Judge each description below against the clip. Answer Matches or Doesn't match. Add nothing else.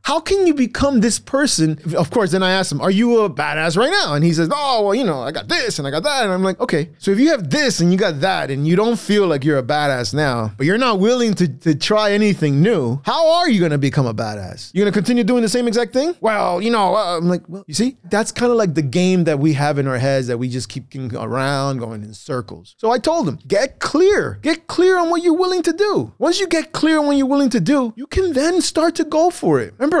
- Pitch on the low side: Doesn't match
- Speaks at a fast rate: Matches